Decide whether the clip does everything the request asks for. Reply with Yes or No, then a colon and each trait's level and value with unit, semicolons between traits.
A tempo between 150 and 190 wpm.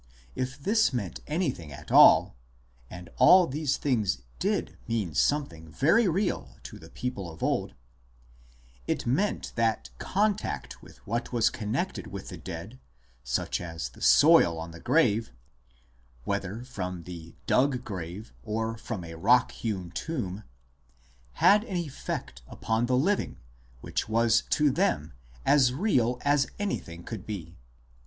No: average, 140 wpm